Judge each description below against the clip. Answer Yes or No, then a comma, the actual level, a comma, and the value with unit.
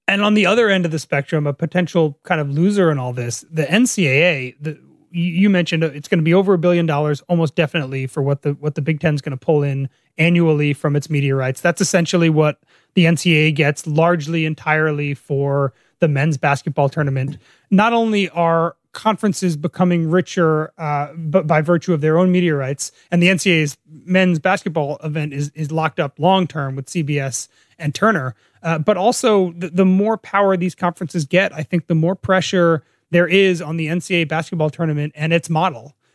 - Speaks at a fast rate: No, average, 190 wpm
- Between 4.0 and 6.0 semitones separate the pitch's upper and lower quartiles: No, average, 3.4 semitones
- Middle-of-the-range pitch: Yes, medium, 165 Hz